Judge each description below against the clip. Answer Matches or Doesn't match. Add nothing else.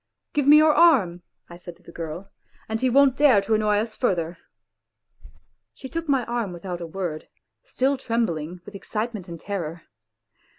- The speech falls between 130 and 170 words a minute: Doesn't match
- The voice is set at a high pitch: Matches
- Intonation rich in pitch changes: Matches